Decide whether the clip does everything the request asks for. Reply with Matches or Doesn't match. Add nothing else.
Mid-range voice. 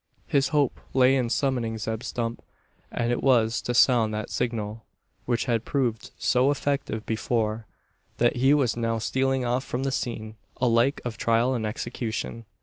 Doesn't match